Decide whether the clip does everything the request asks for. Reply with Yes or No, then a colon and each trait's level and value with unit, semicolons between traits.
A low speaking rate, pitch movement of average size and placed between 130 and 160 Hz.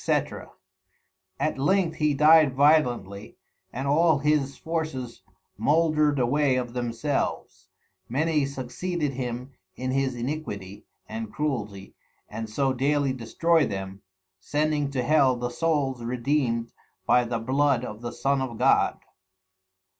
Yes: slow, 125 wpm; average, 3.9 semitones; low, 135 Hz